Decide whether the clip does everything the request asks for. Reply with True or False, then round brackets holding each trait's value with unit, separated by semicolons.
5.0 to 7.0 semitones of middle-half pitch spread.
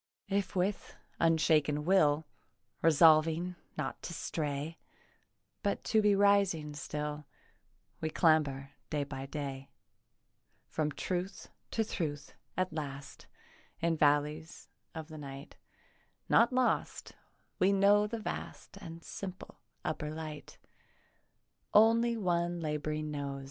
False (3.8 semitones)